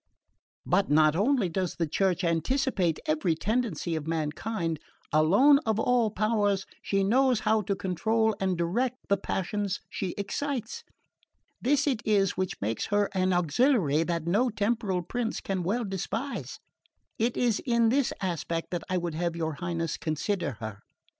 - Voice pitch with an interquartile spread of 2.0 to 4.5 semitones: No, average, 5.0 semitones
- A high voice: Yes, high, 195 Hz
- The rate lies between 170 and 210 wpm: No, average, 155 wpm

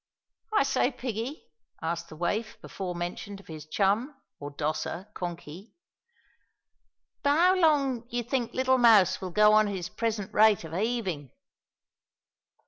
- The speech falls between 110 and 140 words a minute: Yes, slow, 135 wpm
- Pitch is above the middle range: Yes, high, 210 Hz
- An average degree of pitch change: No, wide, 5.8 semitones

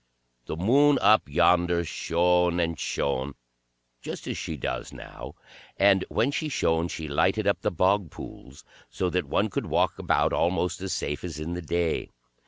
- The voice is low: Yes, very low, 90 Hz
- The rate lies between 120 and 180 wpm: Yes, average, 170 wpm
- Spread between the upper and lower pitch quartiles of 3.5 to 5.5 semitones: No, average, 2.8 semitones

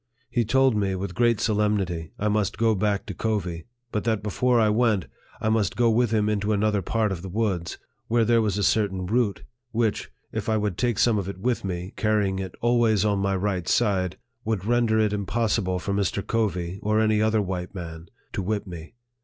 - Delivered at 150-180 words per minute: No, fast, 205 wpm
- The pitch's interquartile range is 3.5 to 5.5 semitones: No, narrow, 2.6 semitones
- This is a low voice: Yes, low, 105 Hz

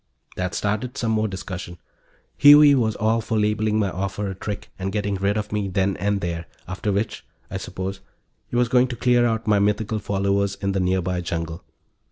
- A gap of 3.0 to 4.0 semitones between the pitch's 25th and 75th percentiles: No, narrow, 2.4 semitones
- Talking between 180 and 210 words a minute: Yes, average, 195 wpm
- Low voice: Yes, low, 100 Hz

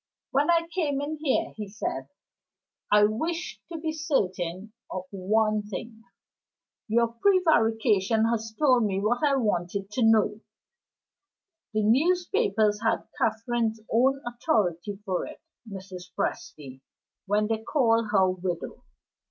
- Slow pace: Yes, slow, 125 wpm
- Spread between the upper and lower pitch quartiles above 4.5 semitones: Yes, average, 4.9 semitones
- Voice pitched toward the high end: Yes, high, 220 Hz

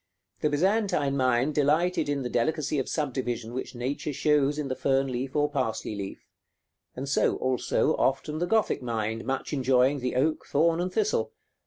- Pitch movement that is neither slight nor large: Yes, average, 3.1 semitones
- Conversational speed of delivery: Yes, average, 170 wpm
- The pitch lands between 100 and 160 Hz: Yes, medium, 140 Hz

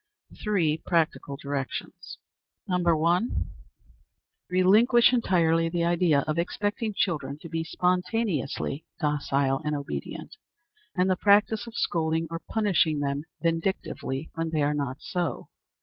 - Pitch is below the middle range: No, medium, 165 Hz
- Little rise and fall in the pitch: No, average, 3.8 semitones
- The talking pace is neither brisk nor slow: No, slow, 120 wpm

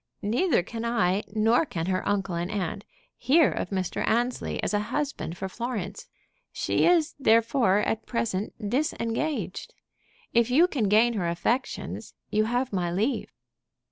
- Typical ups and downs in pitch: Yes, average, 4.2 semitones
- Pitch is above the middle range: Yes, high, 220 Hz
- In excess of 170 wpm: No, average, 145 wpm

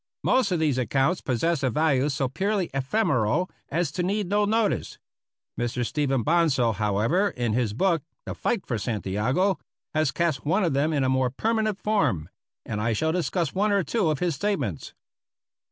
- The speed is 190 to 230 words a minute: No, average, 175 wpm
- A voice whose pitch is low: No, medium, 155 Hz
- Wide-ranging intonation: Yes, wide, 6.9 semitones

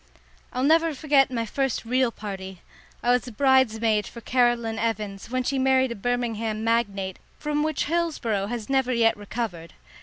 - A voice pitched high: Yes, high, 235 Hz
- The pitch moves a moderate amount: Yes, average, 3.4 semitones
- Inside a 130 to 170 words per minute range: Yes, average, 155 wpm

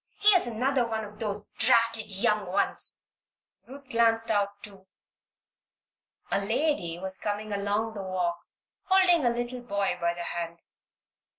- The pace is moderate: No, slow, 130 wpm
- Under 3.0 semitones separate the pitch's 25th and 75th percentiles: No, average, 3.4 semitones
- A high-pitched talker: Yes, high, 210 Hz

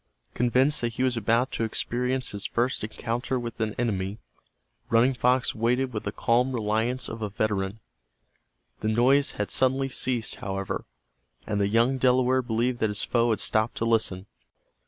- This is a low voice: Yes, low, 115 Hz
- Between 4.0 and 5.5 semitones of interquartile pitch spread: No, average, 2.7 semitones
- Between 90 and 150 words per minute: No, average, 165 wpm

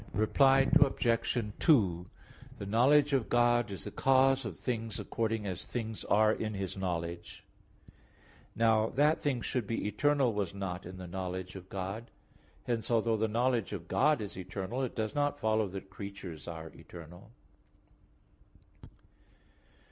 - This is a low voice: Yes, low, 110 Hz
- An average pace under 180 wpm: Yes, average, 145 wpm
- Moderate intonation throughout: Yes, average, 4.4 semitones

